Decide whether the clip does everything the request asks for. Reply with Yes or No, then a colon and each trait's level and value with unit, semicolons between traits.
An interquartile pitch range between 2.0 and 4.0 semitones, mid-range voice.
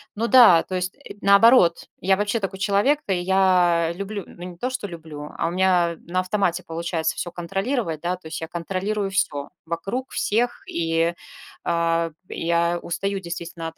Yes: average, 2.9 semitones; medium, 180 Hz